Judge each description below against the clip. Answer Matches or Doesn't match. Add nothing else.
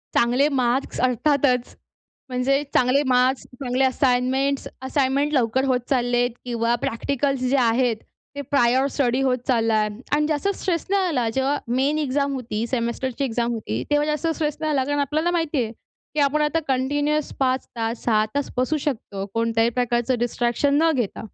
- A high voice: Matches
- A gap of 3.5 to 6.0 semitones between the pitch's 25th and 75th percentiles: Doesn't match